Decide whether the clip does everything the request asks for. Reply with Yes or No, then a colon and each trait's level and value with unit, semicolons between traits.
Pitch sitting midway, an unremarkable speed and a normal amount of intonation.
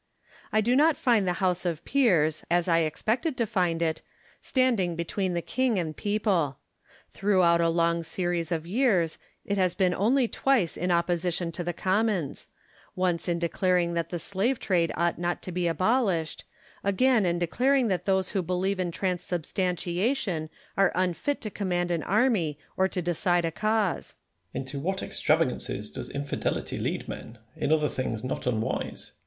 Yes: medium, 180 Hz; average, 165 wpm; average, 3.3 semitones